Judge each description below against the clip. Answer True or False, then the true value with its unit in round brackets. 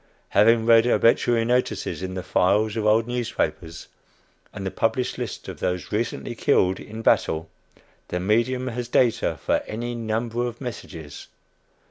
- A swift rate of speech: False (145 wpm)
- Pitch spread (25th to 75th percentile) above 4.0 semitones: False (3.3 semitones)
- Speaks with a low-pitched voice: True (115 Hz)